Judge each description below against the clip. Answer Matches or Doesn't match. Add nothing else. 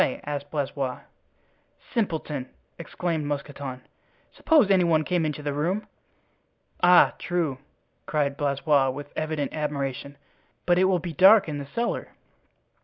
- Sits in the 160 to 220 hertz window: Doesn't match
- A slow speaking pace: Matches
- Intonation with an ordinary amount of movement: Matches